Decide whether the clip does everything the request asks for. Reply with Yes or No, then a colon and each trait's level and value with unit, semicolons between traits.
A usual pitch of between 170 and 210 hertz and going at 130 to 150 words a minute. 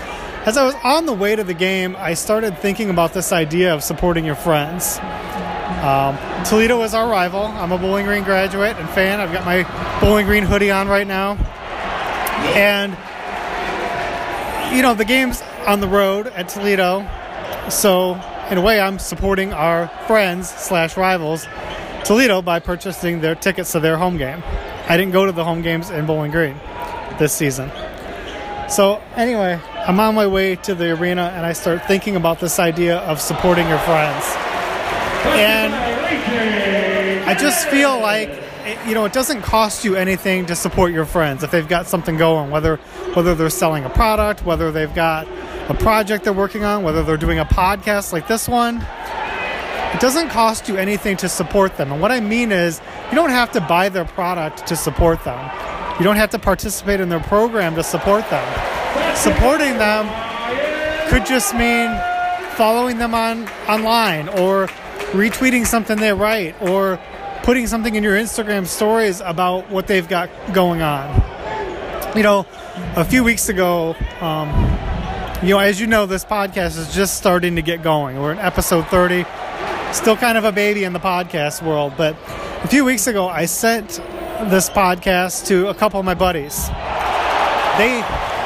No: high, 190 Hz; average, 175 wpm